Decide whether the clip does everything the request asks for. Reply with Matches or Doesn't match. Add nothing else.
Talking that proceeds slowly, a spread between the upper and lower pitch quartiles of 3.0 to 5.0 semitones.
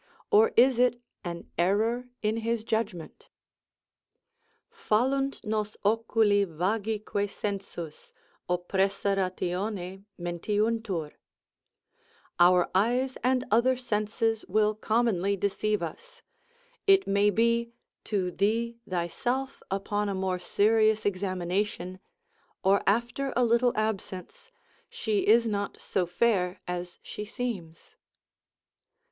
Matches